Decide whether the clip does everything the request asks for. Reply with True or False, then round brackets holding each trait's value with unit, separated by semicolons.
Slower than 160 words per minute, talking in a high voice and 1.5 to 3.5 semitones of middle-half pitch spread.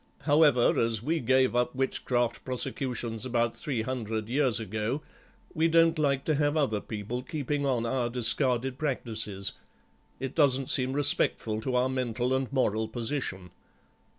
False (145 wpm; 125 Hz; 3.1 semitones)